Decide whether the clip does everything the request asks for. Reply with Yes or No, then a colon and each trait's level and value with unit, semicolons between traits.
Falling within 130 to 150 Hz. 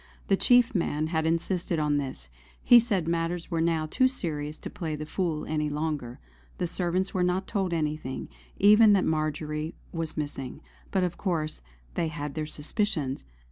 No: medium, 160 Hz